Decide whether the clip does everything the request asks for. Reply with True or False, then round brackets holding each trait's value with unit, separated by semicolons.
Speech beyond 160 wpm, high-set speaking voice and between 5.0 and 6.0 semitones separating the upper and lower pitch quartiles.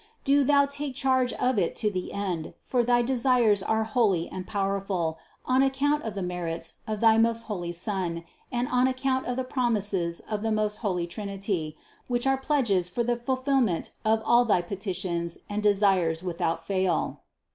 True (180 wpm; 215 Hz; 5.3 semitones)